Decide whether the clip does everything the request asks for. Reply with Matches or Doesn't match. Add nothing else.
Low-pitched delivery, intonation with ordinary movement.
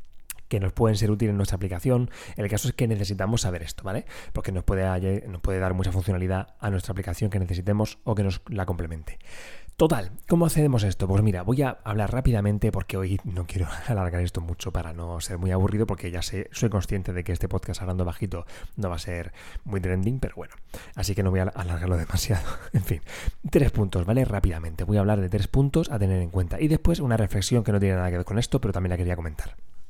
Matches